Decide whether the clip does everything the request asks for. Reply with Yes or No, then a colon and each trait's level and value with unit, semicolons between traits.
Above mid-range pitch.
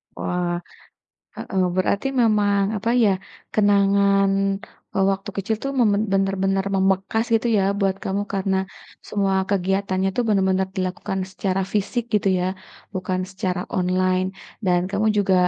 Yes: high, 195 Hz